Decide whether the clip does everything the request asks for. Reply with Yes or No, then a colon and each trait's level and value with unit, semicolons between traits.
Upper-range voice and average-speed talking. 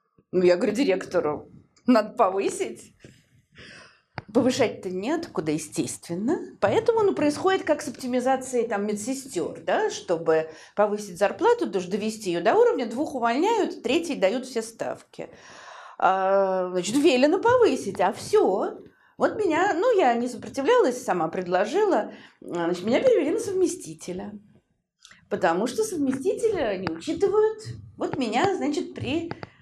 Yes: very high, 265 Hz; average, 120 wpm